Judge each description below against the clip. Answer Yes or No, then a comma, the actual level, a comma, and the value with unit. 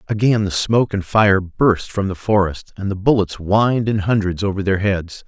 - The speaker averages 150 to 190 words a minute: No, fast, 205 wpm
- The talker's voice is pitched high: No, low, 100 Hz